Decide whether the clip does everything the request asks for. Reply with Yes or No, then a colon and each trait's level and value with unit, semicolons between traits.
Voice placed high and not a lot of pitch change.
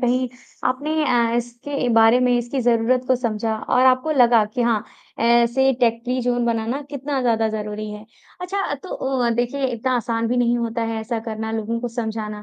Yes: high, 240 Hz; narrow, 2.1 semitones